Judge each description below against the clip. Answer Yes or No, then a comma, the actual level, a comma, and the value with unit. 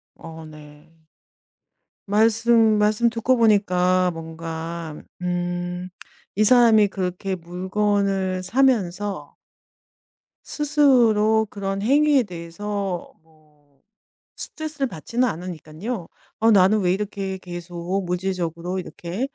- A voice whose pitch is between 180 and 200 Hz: Yes, high, 190 Hz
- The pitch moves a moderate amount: Yes, average, 3.9 semitones